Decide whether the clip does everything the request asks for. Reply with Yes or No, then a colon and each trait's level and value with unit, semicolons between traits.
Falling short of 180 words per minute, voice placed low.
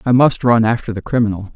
No: fast, 230 wpm; low, 115 Hz